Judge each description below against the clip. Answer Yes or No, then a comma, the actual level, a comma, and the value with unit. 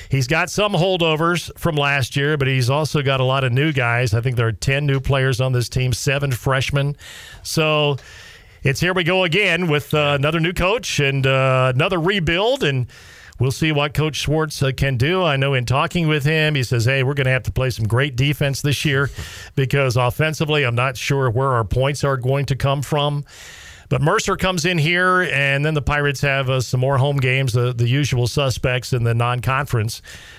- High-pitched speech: No, medium, 140 Hz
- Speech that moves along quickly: Yes, fast, 215 wpm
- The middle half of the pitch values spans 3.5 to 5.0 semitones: No, average, 2.7 semitones